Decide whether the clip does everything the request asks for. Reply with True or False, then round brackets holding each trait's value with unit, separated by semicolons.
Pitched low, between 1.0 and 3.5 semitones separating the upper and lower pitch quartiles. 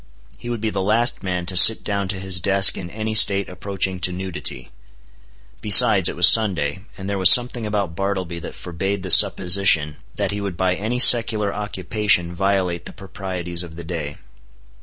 True (95 Hz; 2.6 semitones)